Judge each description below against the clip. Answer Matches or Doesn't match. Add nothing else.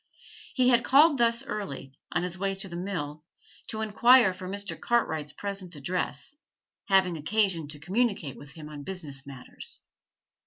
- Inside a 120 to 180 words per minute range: Matches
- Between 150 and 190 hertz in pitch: Matches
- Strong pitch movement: Matches